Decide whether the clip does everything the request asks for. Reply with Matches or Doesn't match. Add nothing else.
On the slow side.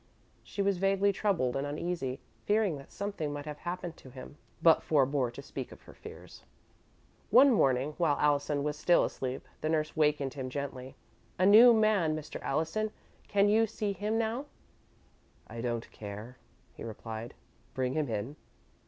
Doesn't match